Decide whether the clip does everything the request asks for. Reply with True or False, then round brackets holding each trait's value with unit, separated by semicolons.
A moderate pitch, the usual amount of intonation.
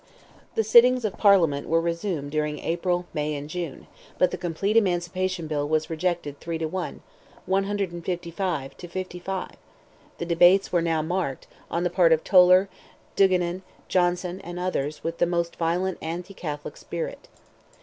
False (175 Hz; 2.3 semitones)